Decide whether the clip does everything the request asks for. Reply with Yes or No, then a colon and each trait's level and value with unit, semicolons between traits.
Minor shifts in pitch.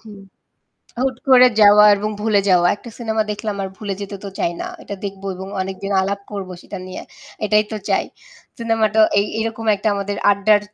Yes: narrow, 1.9 semitones